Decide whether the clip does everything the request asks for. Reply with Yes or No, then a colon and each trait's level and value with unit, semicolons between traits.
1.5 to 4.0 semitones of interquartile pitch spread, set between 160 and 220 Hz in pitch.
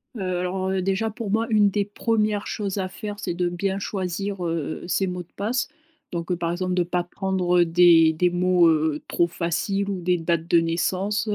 Yes: narrow, 2.5 semitones; medium, 185 Hz